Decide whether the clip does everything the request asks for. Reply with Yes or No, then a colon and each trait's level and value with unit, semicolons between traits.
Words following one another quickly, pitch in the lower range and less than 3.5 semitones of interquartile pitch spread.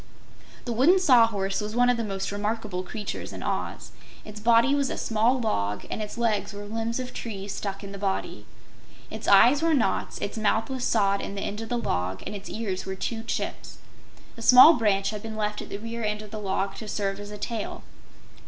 No: fast, 220 wpm; high, 215 Hz; average, 2.7 semitones